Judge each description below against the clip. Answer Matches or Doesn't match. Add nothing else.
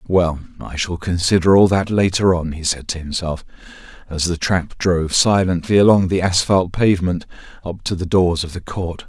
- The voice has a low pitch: Matches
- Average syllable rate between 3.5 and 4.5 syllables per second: Doesn't match